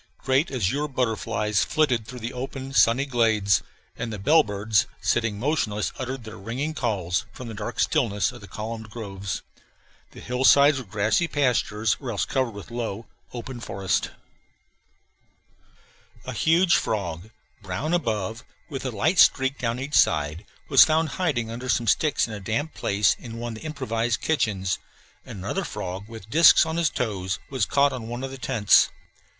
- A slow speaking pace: No, average, 165 wpm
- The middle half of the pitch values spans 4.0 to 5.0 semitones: Yes, average, 4.3 semitones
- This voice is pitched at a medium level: No, low, 115 Hz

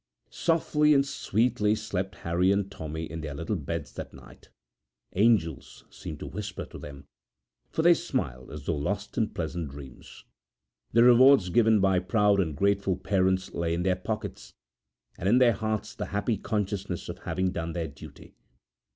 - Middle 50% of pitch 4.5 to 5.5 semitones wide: Yes, average, 4.8 semitones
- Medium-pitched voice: No, very low, 95 Hz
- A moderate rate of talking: Yes, average, 165 wpm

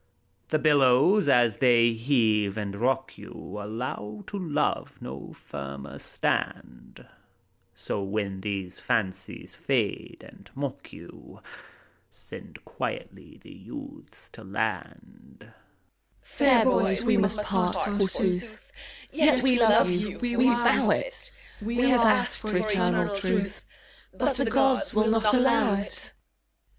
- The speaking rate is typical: No, slow, 125 wpm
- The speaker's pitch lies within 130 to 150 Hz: No, high, 195 Hz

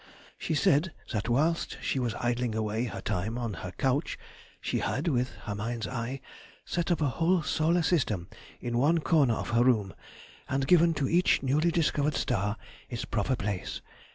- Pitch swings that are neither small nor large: No, wide, 5.7 semitones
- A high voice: No, low, 125 Hz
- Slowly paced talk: No, average, 165 wpm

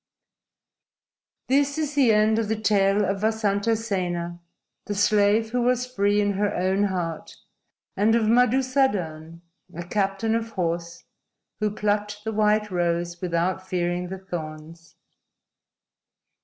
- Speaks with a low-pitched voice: No, high, 205 Hz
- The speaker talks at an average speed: No, slow, 130 wpm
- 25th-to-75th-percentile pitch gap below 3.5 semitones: No, average, 3.9 semitones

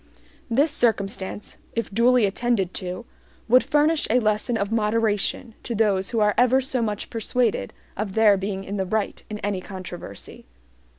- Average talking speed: Yes, average, 160 wpm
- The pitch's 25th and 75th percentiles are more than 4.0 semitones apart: No, average, 3.4 semitones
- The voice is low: No, high, 215 Hz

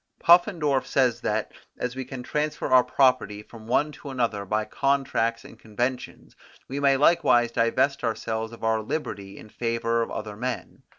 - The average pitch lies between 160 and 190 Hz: No, low, 120 Hz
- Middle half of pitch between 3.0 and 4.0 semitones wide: Yes, average, 3.5 semitones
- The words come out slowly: No, average, 165 wpm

